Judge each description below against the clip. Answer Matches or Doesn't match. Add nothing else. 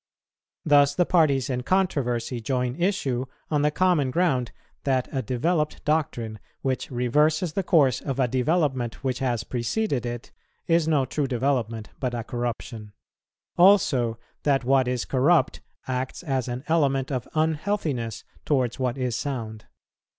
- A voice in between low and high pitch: Doesn't match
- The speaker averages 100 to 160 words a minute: Matches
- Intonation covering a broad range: Doesn't match